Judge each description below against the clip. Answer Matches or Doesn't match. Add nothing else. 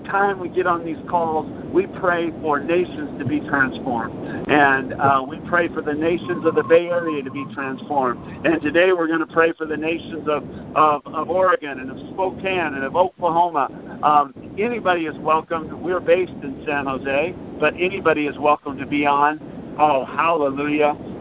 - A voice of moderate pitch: Matches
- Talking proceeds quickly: Doesn't match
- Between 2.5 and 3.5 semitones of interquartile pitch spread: Matches